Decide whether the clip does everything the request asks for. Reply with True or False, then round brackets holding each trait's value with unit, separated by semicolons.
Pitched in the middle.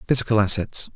False (110 Hz)